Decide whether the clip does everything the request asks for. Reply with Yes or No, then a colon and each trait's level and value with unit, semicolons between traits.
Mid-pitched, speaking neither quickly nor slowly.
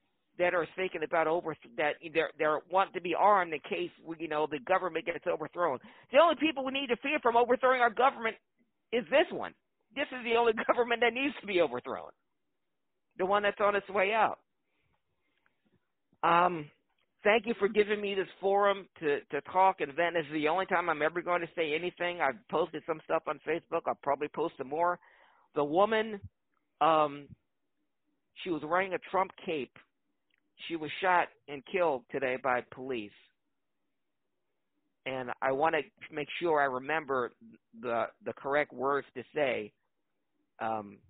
Yes: medium, 175 Hz; average, 170 wpm